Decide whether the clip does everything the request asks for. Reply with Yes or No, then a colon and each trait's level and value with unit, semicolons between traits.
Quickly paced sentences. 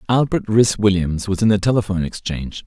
No: average, 180 wpm